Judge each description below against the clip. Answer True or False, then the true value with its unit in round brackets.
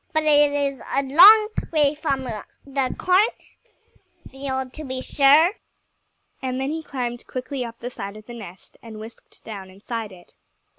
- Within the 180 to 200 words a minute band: False (155 wpm)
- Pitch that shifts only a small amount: False (4.0 semitones)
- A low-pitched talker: False (265 Hz)